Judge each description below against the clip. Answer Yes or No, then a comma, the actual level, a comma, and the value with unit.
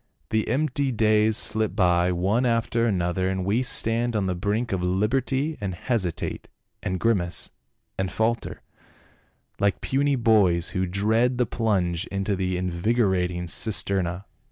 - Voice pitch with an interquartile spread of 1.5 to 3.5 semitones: No, average, 4.1 semitones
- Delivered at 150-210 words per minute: No, average, 140 wpm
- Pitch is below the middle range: Yes, low, 100 Hz